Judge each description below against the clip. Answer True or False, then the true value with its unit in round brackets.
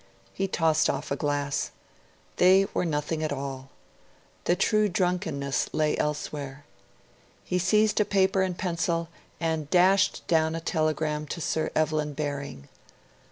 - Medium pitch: True (160 Hz)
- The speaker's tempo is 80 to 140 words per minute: True (135 wpm)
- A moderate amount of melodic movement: True (3.5 semitones)